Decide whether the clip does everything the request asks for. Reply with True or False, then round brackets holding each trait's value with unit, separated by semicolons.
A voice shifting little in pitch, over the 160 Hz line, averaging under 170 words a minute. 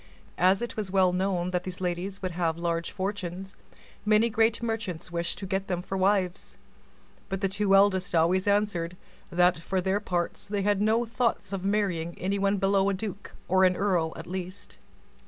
False (2.1 semitones; 190 Hz; 185 wpm)